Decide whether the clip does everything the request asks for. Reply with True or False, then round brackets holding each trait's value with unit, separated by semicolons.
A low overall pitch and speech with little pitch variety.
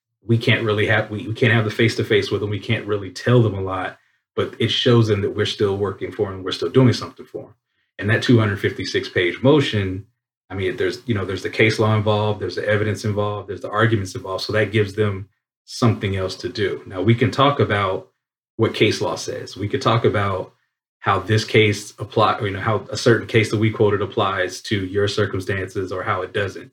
True (105 Hz; 2.2 semitones)